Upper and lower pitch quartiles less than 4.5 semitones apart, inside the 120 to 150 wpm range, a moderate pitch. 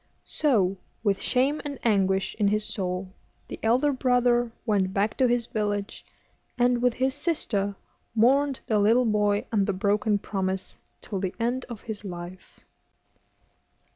No: average, 3.9 semitones; average, 145 wpm; high, 215 Hz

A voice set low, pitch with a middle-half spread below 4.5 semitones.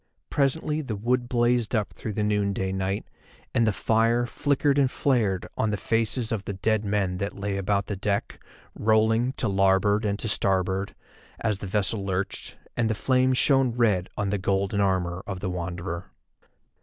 Yes: low, 105 Hz; average, 3.4 semitones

